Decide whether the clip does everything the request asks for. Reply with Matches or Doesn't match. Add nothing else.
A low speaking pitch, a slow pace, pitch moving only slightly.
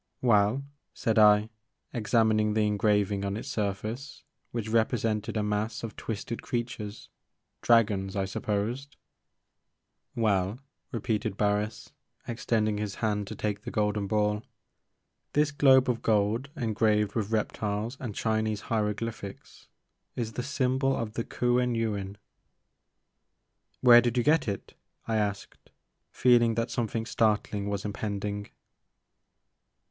Matches